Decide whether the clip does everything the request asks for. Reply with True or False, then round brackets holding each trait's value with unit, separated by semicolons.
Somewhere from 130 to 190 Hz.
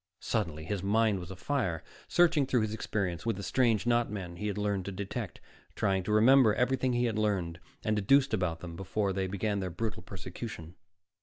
False (105 Hz)